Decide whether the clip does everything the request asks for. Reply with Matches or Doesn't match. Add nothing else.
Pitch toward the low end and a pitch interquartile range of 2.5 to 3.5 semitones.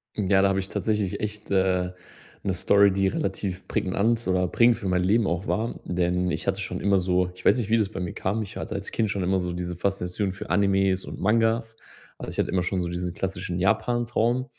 Matches